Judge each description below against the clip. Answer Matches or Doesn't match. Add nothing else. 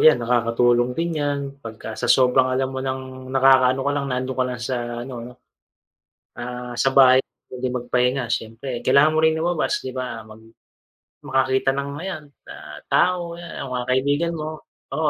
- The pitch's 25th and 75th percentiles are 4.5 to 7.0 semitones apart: Doesn't match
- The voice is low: Matches